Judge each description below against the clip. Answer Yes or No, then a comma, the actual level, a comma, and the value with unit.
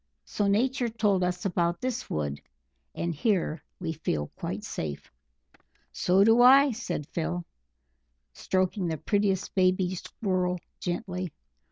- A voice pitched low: No, medium, 185 Hz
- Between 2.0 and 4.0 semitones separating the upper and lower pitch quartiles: Yes, average, 3.4 semitones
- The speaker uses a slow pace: Yes, slow, 125 wpm